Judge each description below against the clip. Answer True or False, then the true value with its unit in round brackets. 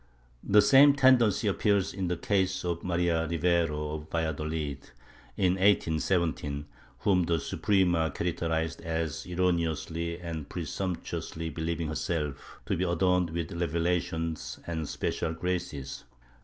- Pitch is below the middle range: True (85 Hz)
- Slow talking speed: True (120 wpm)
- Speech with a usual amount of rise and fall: False (2.2 semitones)